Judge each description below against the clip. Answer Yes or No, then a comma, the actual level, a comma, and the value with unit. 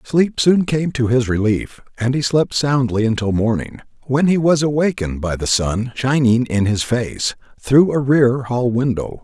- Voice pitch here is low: Yes, low, 125 Hz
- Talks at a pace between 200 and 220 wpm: No, average, 180 wpm